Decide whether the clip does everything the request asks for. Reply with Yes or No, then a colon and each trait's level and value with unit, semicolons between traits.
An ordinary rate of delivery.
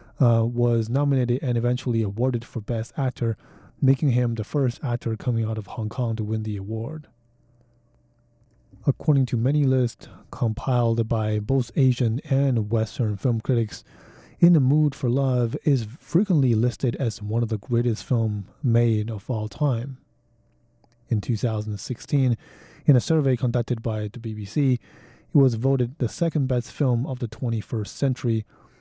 Yes: average, 150 wpm